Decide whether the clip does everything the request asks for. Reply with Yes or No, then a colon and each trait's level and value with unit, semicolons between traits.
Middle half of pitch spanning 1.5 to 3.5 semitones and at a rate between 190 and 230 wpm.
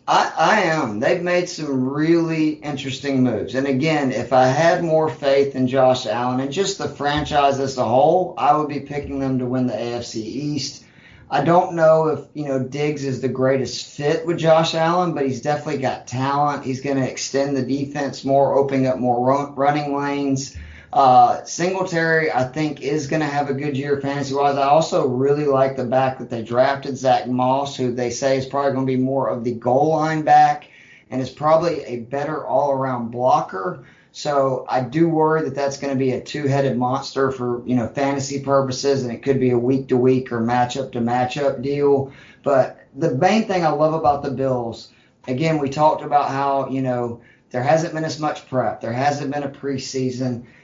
Yes: narrow, 2.4 semitones; fast, 205 wpm